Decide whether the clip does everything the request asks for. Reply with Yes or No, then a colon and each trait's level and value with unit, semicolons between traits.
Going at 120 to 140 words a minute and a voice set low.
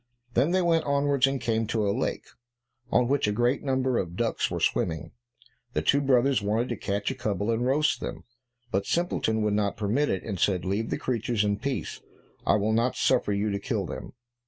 No: fast, 205 wpm; low, 115 Hz